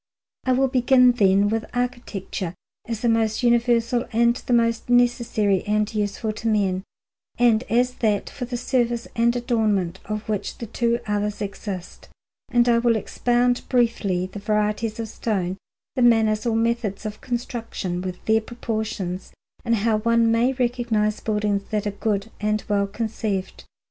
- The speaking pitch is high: Yes, high, 225 Hz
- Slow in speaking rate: No, average, 155 wpm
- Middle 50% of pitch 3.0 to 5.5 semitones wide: No, narrow, 2.4 semitones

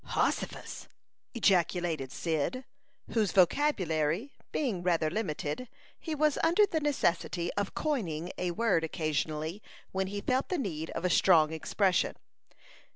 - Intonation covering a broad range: Yes, wide, 7.0 semitones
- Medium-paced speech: No, slow, 125 wpm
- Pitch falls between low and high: Yes, medium, 180 Hz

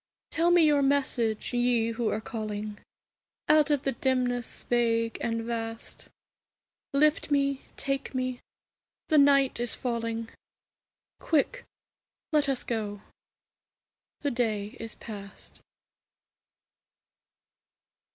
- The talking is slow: Yes, slow, 105 wpm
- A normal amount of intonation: Yes, average, 3.6 semitones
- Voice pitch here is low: No, high, 245 Hz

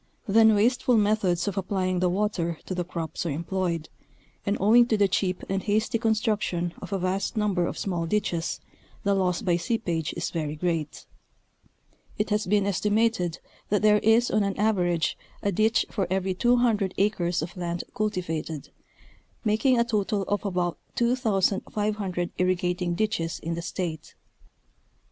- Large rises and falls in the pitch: No, average, 3.4 semitones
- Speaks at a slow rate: No, average, 155 wpm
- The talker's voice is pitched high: Yes, high, 195 Hz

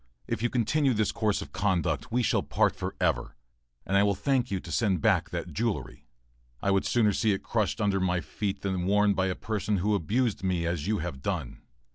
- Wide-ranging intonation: No, average, 2.9 semitones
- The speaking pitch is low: Yes, low, 100 Hz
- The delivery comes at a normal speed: No, fast, 210 wpm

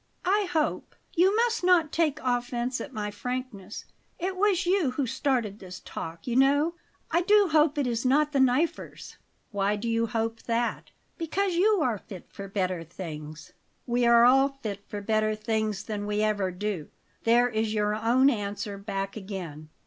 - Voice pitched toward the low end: No, high, 235 Hz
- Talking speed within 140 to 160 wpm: No, average, 170 wpm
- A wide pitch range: Yes, wide, 5.9 semitones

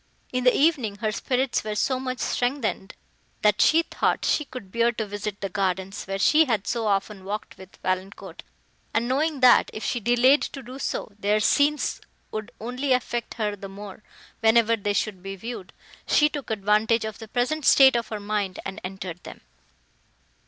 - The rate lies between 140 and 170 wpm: No, average, 180 wpm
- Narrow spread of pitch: No, average, 4.0 semitones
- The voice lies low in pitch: No, high, 220 Hz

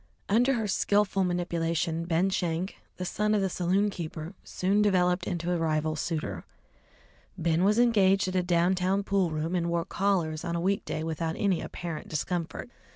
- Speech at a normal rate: Yes, average, 170 wpm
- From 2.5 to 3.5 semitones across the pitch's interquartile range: Yes, average, 2.9 semitones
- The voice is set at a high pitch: No, medium, 180 Hz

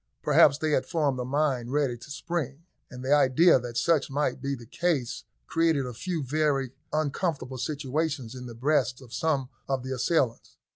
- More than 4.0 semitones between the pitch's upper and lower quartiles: No, average, 3.4 semitones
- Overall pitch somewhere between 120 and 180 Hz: Yes, medium, 140 Hz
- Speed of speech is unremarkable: Yes, average, 180 wpm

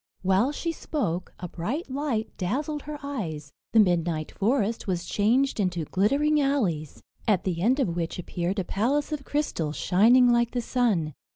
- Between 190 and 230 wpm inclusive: No, average, 165 wpm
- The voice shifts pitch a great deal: Yes, wide, 7.7 semitones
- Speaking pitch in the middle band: No, high, 215 Hz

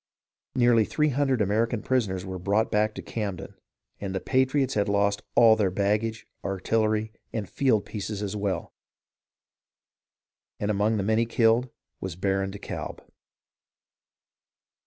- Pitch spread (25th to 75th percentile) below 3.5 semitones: Yes, narrow, 2.4 semitones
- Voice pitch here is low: Yes, low, 105 Hz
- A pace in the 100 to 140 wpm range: Yes, slow, 135 wpm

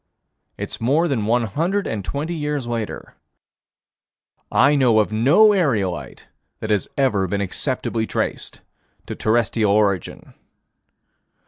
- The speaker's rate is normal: No, slow, 120 wpm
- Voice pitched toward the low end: Yes, low, 120 Hz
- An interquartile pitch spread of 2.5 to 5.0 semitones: No, wide, 5.5 semitones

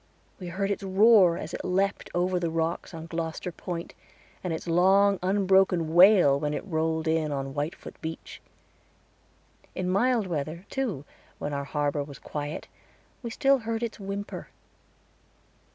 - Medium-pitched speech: Yes, medium, 175 Hz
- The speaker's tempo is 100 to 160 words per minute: Yes, average, 150 wpm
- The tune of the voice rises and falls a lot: No, average, 3.7 semitones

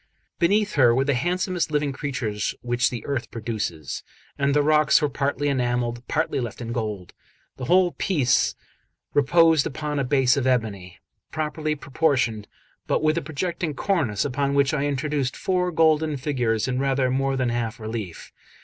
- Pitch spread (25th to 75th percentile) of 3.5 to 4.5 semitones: Yes, average, 4.1 semitones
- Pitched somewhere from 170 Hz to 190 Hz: No, medium, 140 Hz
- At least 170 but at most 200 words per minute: No, average, 160 wpm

